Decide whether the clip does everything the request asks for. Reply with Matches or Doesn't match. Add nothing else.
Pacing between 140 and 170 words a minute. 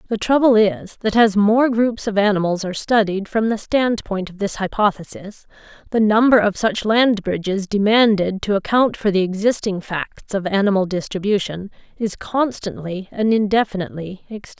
Matches